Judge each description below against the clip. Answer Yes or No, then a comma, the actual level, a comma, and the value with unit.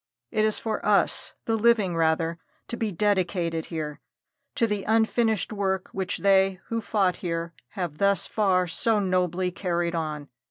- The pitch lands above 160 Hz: Yes, high, 190 Hz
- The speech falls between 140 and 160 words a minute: Yes, average, 155 wpm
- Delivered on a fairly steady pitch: No, average, 3.8 semitones